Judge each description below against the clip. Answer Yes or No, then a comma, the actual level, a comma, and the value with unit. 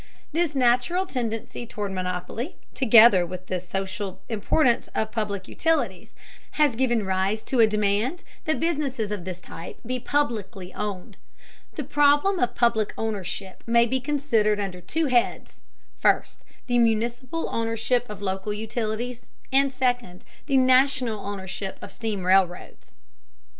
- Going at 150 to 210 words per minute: No, slow, 135 wpm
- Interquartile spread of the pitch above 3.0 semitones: Yes, average, 4.6 semitones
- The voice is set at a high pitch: Yes, high, 225 Hz